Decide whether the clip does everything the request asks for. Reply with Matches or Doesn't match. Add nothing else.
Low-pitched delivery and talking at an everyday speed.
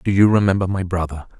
Doesn't match